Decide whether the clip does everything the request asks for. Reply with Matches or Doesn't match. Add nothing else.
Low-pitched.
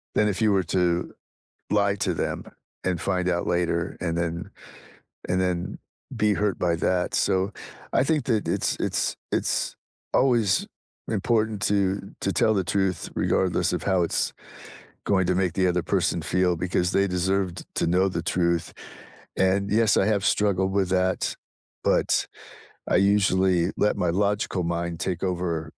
Matches